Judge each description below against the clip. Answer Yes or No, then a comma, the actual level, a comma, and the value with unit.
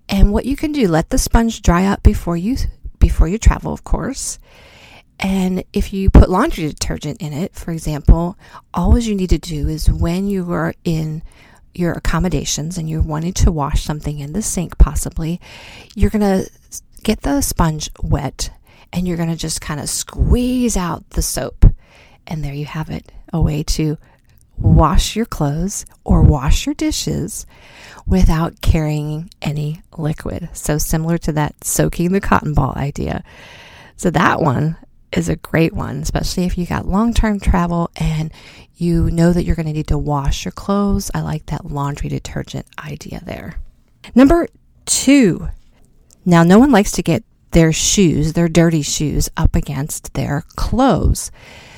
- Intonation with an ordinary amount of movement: Yes, average, 4.2 semitones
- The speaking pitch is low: No, medium, 165 Hz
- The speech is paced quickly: No, average, 165 wpm